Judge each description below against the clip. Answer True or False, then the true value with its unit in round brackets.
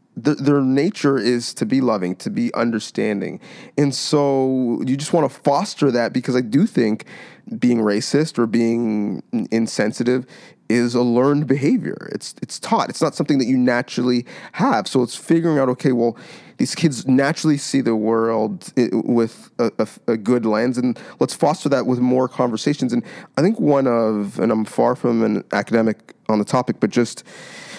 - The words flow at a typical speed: True (175 wpm)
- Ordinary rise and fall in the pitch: True (3.2 semitones)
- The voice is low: True (125 Hz)